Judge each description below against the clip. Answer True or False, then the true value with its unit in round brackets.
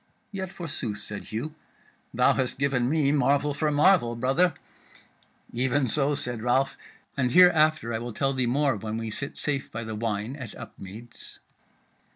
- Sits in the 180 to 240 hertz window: False (130 Hz)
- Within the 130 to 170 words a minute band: True (160 wpm)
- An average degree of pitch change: True (4.0 semitones)